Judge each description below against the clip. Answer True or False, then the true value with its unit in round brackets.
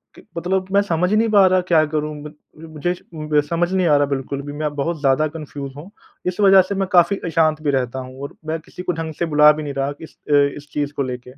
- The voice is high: False (155 Hz)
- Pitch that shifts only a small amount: False (3.8 semitones)